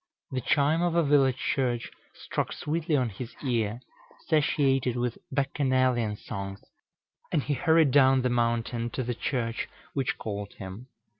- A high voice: No, low, 130 Hz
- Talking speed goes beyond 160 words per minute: No, average, 145 wpm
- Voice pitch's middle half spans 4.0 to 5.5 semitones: No, average, 3.2 semitones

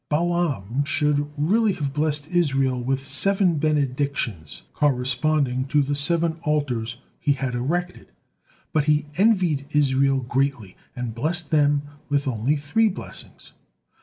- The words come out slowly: Yes, slow, 125 wpm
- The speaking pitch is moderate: Yes, medium, 145 Hz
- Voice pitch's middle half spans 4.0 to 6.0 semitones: No, average, 2.9 semitones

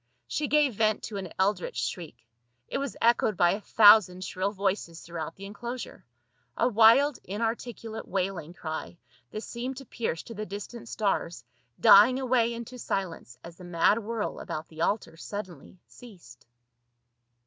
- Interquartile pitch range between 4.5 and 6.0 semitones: Yes, average, 4.8 semitones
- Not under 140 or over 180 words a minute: Yes, average, 150 wpm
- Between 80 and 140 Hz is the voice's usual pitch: No, high, 205 Hz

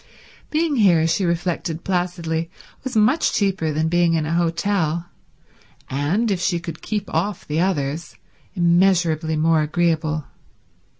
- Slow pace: Yes, slow, 130 wpm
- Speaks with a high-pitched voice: No, medium, 170 Hz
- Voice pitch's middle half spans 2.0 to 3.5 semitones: Yes, average, 3.1 semitones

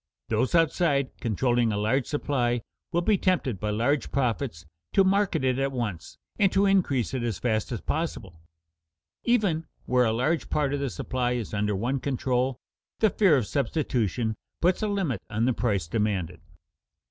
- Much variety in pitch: Yes, wide, 5.9 semitones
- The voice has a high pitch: No, low, 130 Hz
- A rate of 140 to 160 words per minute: No, average, 170 wpm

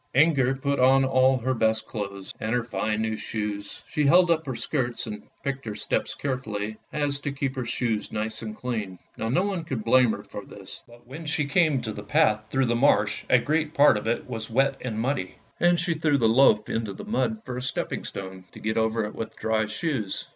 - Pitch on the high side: No, low, 120 Hz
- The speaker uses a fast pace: Yes, fast, 225 wpm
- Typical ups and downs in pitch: Yes, average, 4.3 semitones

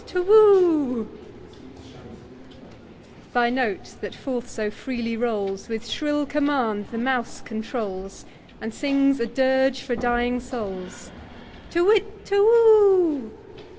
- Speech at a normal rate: No, slow, 105 wpm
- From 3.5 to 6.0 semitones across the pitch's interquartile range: Yes, average, 4.2 semitones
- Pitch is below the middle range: No, high, 245 Hz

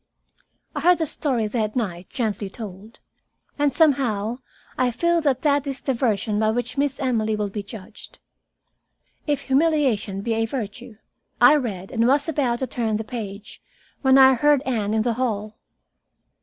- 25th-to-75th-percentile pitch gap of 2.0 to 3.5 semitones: No, average, 4.3 semitones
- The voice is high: Yes, high, 240 Hz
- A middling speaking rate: Yes, average, 170 wpm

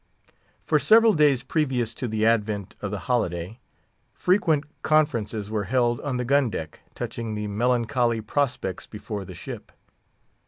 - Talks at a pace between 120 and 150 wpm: Yes, average, 145 wpm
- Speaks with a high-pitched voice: No, low, 120 Hz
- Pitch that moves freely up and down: No, average, 4.5 semitones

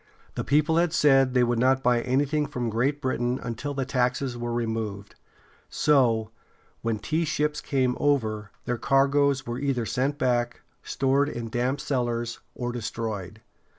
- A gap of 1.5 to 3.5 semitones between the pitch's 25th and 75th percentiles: Yes, average, 2.9 semitones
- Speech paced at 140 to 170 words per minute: Yes, average, 150 wpm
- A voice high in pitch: No, low, 125 Hz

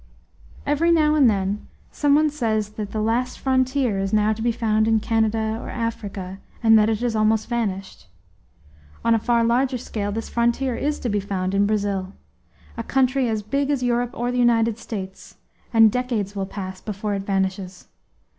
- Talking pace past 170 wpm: Yes, average, 185 wpm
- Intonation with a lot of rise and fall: No, average, 3.2 semitones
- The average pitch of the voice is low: No, high, 225 Hz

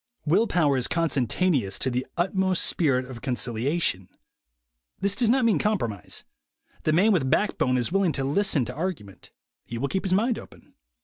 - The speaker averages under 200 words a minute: Yes, average, 175 wpm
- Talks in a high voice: No, medium, 155 Hz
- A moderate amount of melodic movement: No, wide, 7.0 semitones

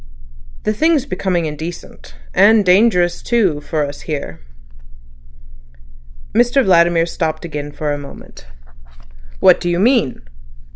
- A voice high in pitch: No, medium, 175 Hz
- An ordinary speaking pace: No, slow, 115 wpm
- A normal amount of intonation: No, wide, 6.1 semitones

